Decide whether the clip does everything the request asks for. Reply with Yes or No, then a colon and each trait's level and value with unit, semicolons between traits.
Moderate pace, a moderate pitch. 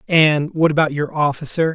Yes: average, 170 wpm; medium, 155 Hz